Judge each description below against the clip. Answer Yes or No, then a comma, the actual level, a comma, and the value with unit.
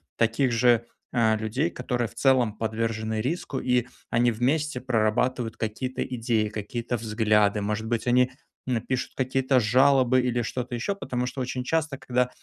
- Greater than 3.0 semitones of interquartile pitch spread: No, narrow, 2.5 semitones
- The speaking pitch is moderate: No, low, 120 Hz